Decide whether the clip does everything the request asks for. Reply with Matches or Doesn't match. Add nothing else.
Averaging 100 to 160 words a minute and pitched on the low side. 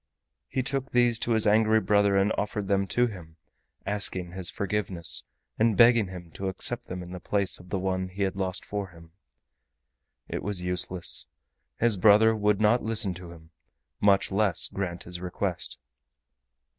Doesn't match